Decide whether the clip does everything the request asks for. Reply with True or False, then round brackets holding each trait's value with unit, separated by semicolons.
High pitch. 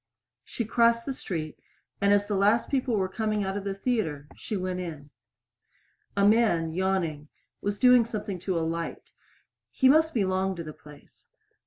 True (195 Hz)